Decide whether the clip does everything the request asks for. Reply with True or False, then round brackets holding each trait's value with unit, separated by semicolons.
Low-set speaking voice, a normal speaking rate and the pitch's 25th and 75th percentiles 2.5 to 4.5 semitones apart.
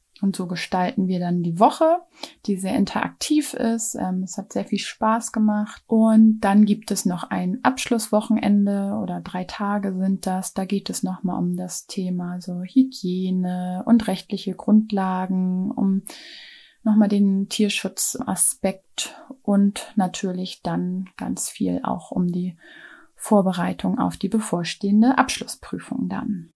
False (200 Hz; 135 wpm; 3.2 semitones)